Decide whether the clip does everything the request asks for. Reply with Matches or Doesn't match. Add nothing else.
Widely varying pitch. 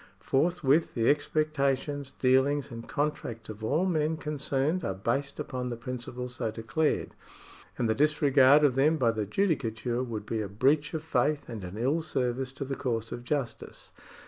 Doesn't match